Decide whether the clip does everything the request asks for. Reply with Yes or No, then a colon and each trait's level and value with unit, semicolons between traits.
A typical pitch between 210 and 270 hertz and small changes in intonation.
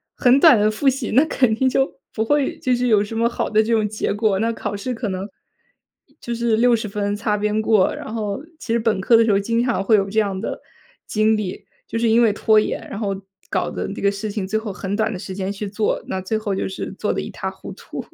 Yes: high, 215 Hz; narrow, 2.3 semitones